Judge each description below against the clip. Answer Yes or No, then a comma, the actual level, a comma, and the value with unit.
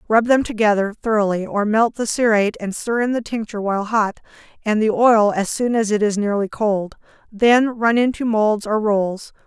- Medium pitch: No, high, 215 Hz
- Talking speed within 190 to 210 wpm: Yes, average, 195 wpm